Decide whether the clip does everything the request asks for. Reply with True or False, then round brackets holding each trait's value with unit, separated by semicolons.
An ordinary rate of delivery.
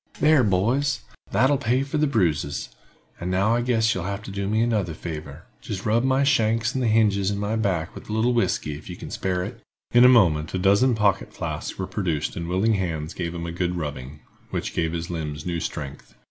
False (215 wpm)